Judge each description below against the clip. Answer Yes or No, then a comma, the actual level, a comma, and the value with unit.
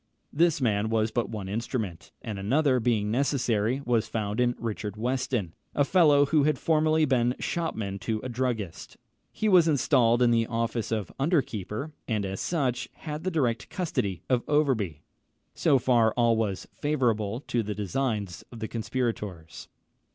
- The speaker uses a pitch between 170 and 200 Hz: No, low, 120 Hz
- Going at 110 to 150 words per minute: No, average, 160 wpm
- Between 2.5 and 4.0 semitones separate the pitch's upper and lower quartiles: No, average, 4.5 semitones